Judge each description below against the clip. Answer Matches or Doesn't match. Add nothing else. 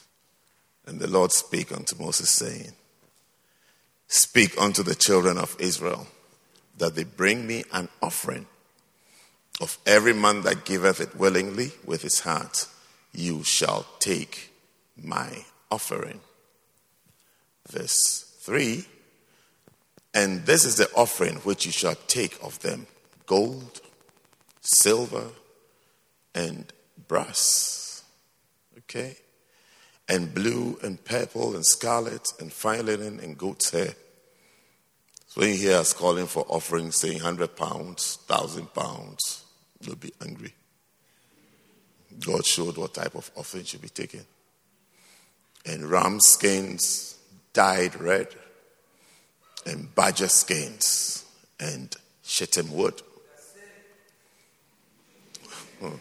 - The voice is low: Matches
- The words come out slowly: Matches